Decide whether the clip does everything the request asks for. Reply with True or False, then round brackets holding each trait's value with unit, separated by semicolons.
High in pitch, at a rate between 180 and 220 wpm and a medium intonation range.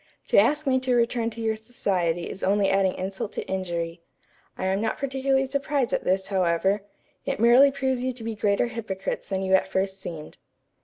True (205 Hz; 195 wpm; 4.7 semitones)